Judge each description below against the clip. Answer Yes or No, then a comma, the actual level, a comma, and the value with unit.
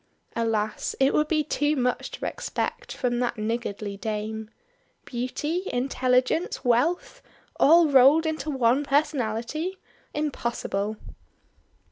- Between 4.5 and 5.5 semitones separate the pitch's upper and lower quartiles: Yes, average, 4.9 semitones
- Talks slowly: Yes, slow, 105 wpm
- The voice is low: No, very high, 255 Hz